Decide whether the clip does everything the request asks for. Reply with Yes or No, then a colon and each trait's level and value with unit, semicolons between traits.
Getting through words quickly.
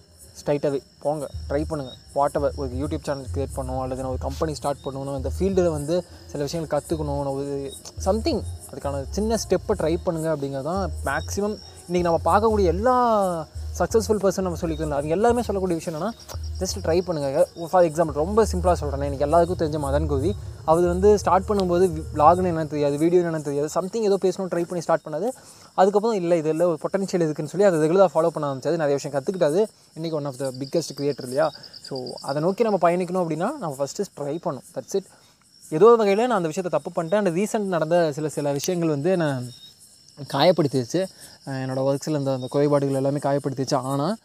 Yes: fast, 180 wpm